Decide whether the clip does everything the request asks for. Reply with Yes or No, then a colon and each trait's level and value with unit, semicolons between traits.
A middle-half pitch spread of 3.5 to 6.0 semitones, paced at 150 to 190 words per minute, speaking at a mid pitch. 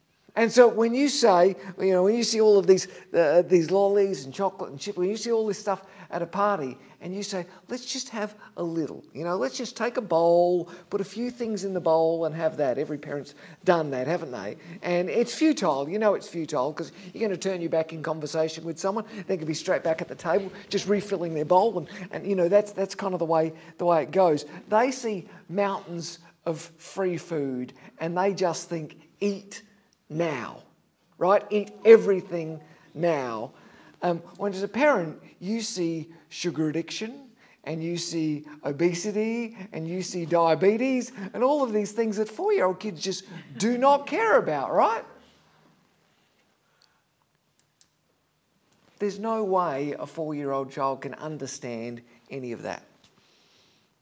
Yes: average, 4.1 semitones; average, 185 wpm; medium, 180 Hz